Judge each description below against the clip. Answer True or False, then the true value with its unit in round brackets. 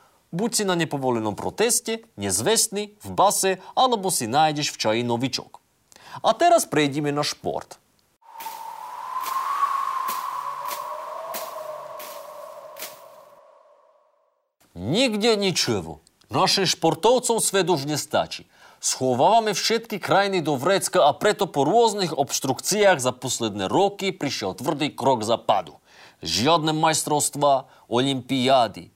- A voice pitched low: False (180 Hz)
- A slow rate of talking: True (95 wpm)